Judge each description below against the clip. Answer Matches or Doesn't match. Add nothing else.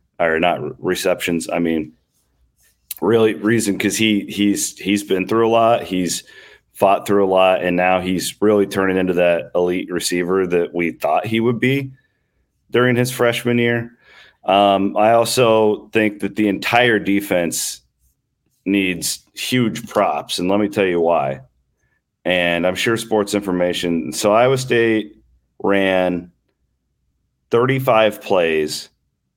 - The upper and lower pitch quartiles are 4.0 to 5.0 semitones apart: Matches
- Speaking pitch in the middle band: Doesn't match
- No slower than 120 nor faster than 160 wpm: Matches